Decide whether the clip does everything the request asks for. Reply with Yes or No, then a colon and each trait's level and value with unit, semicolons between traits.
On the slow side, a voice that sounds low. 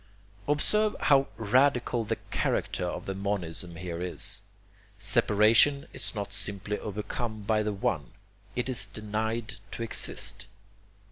Yes: slow, 125 wpm; low, 105 Hz